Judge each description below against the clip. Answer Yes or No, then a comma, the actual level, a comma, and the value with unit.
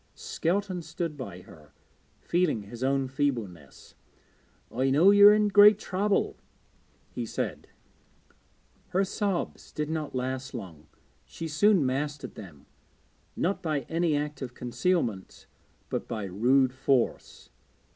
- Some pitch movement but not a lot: No, wide, 6.6 semitones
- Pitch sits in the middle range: Yes, medium, 145 Hz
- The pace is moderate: No, slow, 125 wpm